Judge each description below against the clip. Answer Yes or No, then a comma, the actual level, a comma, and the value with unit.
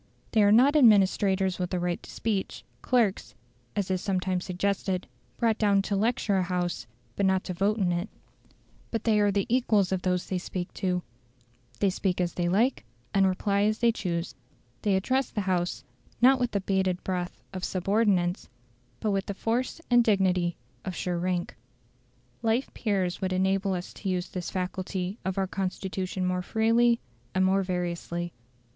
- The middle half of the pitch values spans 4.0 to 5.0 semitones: No, narrow, 2.5 semitones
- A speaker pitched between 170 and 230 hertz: Yes, high, 190 Hz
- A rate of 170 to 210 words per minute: Yes, average, 175 wpm